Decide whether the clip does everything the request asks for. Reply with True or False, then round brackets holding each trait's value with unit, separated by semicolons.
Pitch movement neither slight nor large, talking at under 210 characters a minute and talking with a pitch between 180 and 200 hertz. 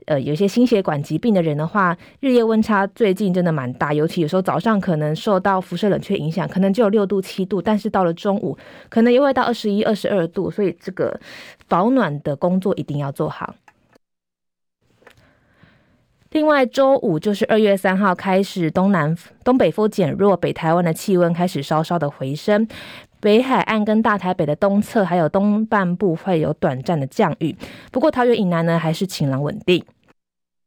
False (4.7 semitones; 285 characters per minute; 190 Hz)